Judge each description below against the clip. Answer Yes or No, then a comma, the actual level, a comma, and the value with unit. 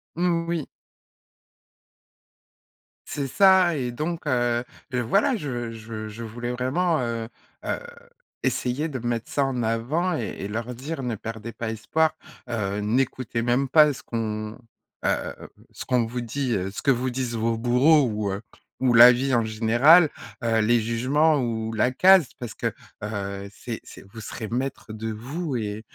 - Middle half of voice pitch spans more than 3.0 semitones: Yes, average, 3.7 semitones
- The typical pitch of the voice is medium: No, low, 120 Hz